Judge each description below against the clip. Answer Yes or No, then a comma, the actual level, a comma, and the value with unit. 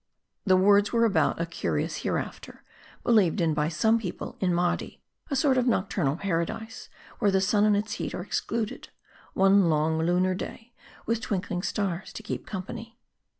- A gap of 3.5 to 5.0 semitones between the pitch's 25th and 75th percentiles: Yes, average, 4.0 semitones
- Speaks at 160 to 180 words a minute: Yes, average, 165 wpm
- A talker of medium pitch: No, high, 195 Hz